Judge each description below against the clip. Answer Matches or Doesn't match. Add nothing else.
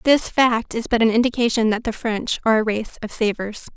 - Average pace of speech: Doesn't match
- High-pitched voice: Matches